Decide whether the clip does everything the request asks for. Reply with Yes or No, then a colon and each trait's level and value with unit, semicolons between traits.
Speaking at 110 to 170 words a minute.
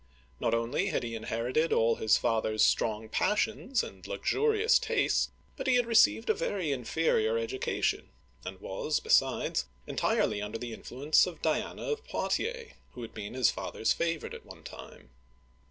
Yes: average, 160 wpm